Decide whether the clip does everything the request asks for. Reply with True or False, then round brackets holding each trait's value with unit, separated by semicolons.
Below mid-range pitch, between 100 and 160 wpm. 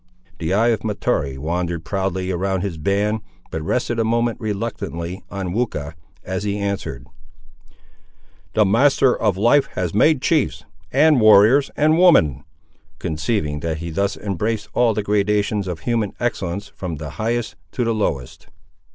True (100 Hz; 150 wpm)